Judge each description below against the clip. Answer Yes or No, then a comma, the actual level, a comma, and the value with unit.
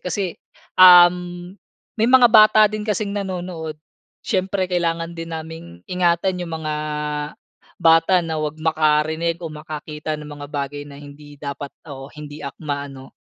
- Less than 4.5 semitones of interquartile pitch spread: Yes, average, 3.1 semitones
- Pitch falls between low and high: Yes, medium, 165 Hz